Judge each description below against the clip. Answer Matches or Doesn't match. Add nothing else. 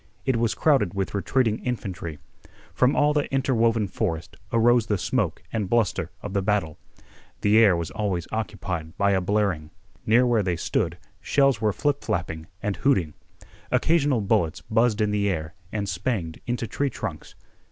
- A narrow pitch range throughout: Doesn't match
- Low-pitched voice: Matches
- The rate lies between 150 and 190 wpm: Matches